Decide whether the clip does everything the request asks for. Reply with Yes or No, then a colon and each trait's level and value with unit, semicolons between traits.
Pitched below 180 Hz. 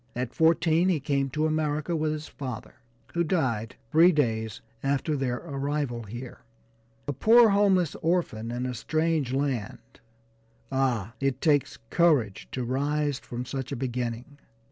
Yes: medium, 140 Hz